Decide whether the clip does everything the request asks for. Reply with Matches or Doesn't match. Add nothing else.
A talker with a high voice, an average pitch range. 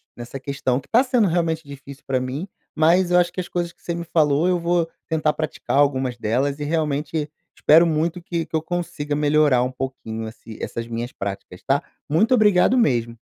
Doesn't match